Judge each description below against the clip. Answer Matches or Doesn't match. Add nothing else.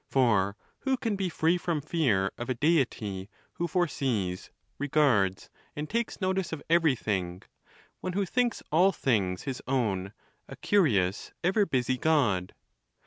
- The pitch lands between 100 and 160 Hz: Matches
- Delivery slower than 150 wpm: Matches